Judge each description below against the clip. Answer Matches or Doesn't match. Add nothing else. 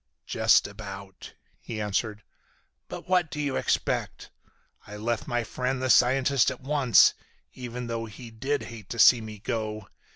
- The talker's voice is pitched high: Doesn't match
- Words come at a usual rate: Matches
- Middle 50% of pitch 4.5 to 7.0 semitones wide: Doesn't match